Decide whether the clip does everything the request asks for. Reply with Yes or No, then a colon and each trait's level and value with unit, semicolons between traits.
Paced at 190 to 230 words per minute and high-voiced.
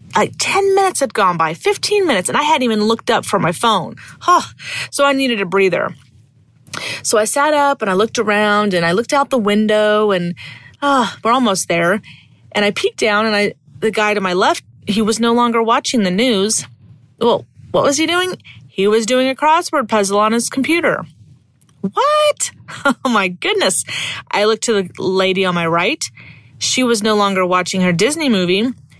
Yes: average, 195 wpm; high, 215 Hz